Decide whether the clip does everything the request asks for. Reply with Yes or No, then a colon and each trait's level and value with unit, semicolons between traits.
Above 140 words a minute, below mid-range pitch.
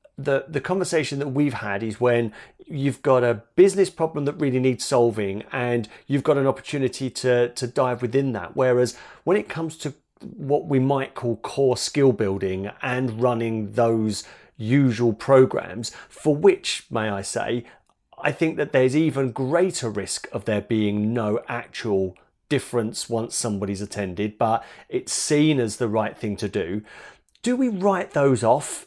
Yes: average, 165 wpm; low, 125 Hz